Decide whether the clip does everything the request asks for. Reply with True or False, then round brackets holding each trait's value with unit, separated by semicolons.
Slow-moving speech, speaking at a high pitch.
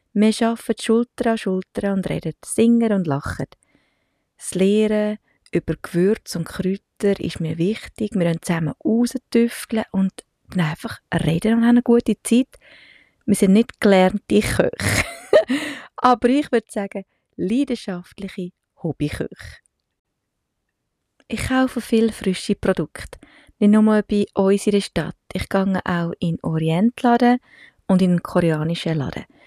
True (130 wpm; 205 Hz)